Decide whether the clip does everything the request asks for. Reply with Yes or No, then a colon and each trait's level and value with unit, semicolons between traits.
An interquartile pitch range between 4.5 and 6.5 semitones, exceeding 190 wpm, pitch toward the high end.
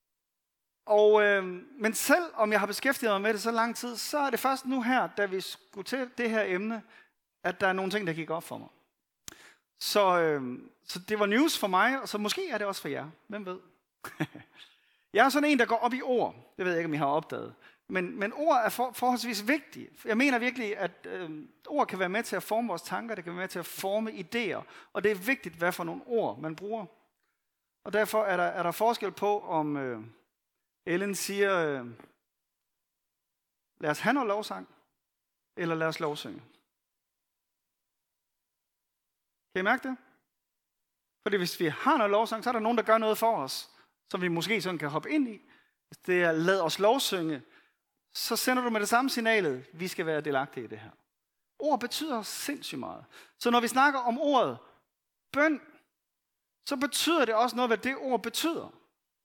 Yes: average, 5.1 semitones; average, 205 wpm; high, 210 Hz